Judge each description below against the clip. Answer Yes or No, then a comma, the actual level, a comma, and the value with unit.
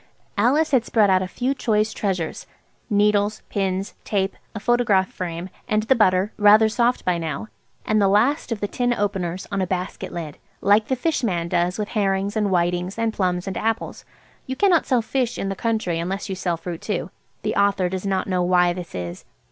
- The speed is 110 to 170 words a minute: No, average, 195 wpm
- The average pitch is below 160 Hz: No, high, 200 Hz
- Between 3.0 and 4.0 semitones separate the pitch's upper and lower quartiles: Yes, average, 3.3 semitones